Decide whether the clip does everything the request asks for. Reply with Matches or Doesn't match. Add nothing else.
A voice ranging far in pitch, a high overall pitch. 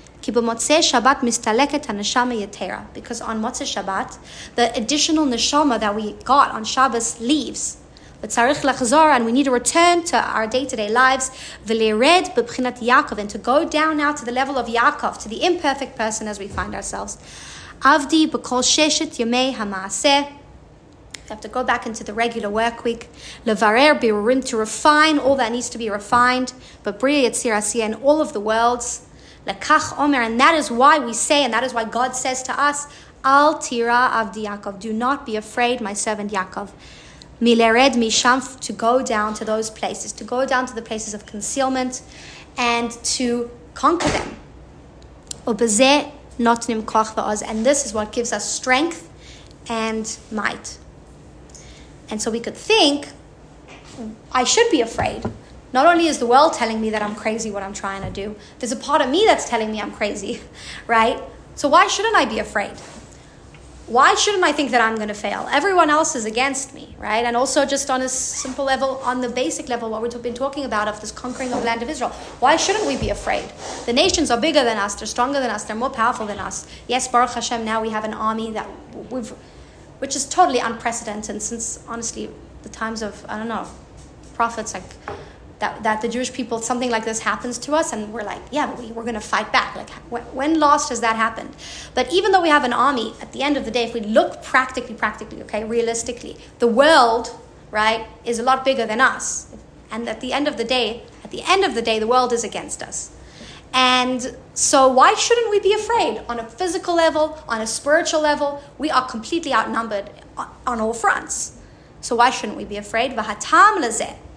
Doesn't match